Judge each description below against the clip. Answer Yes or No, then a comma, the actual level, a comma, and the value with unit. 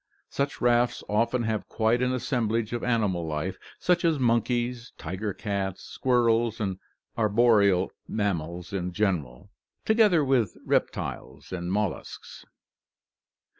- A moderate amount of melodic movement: Yes, average, 4.1 semitones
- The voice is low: Yes, low, 110 Hz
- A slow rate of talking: Yes, slow, 115 wpm